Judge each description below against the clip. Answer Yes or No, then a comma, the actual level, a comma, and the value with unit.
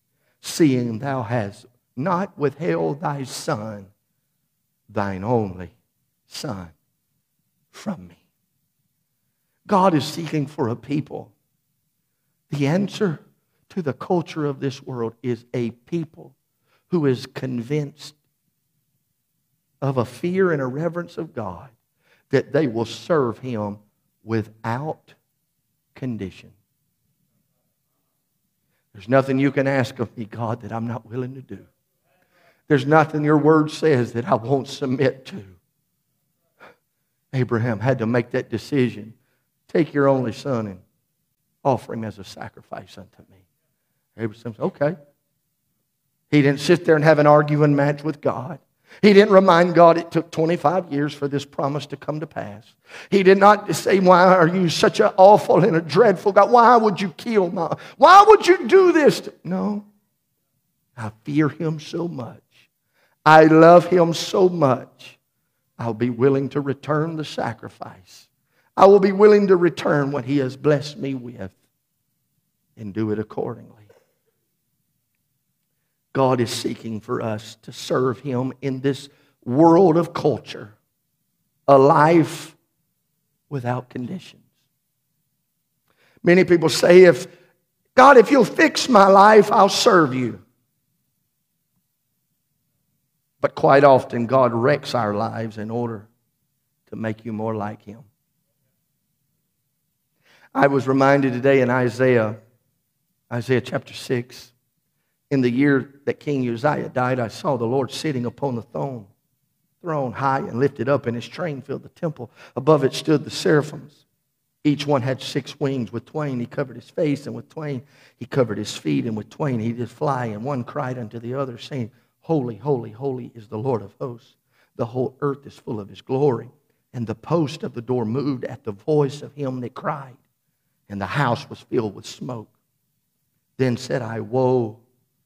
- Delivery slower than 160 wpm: Yes, average, 150 wpm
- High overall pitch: No, medium, 140 Hz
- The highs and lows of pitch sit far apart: No, average, 4.5 semitones